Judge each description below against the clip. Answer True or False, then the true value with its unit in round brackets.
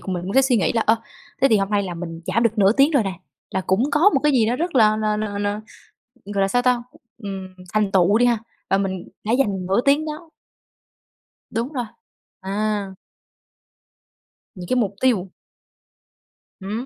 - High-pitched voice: True (215 Hz)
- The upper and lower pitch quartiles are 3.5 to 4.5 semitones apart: True (4.1 semitones)